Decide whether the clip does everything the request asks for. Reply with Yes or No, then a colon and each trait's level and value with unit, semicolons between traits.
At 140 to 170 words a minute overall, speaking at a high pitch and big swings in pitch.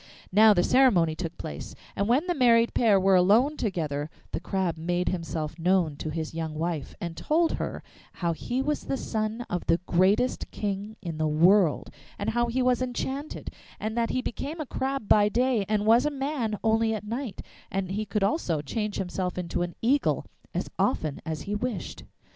No: average, 190 wpm; high, 205 Hz; wide, 5.8 semitones